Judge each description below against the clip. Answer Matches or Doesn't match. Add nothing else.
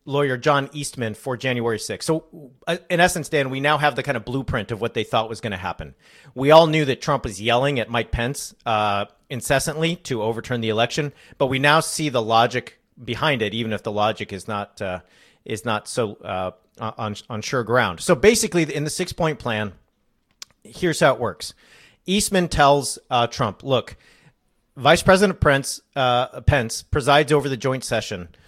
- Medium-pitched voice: Doesn't match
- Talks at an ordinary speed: Matches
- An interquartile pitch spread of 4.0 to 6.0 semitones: Matches